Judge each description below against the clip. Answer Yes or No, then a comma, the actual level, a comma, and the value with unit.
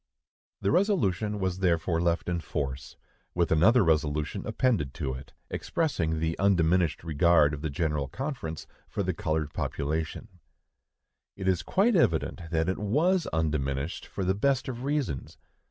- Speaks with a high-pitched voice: No, very low, 85 Hz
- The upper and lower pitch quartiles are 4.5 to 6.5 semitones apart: Yes, average, 4.8 semitones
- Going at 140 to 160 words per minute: Yes, average, 145 wpm